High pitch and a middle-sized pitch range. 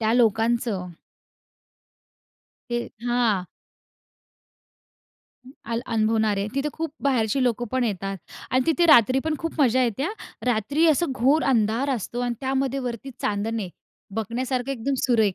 Yes: high, 240 Hz; average, 3.6 semitones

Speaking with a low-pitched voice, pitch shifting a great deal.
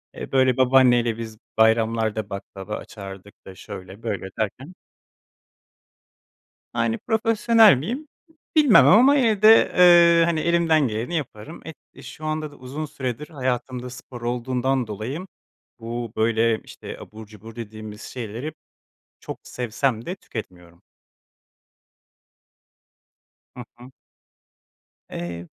Yes: low, 120 Hz; wide, 6.1 semitones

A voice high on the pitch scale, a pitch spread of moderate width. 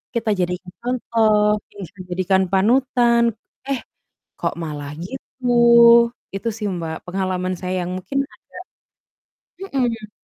Yes: high, 205 Hz; average, 4.4 semitones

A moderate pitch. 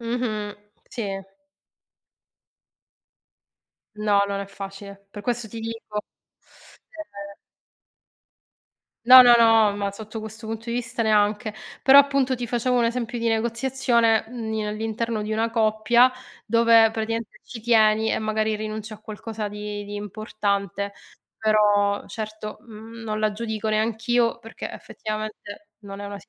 No: high, 220 Hz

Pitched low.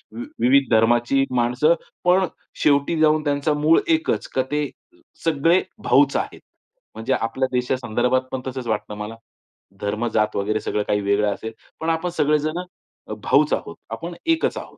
Yes: low, 130 Hz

